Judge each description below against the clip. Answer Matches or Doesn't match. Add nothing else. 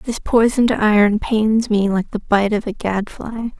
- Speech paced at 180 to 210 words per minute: Matches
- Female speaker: Matches